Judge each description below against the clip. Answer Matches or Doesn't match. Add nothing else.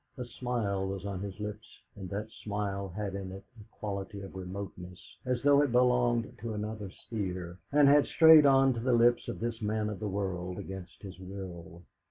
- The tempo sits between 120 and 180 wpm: Doesn't match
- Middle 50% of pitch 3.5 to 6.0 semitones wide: Matches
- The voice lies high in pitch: Doesn't match